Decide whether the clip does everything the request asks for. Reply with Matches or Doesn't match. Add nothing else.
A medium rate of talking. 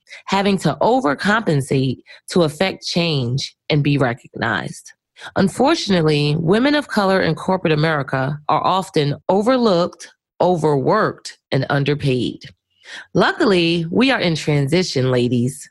Doesn't match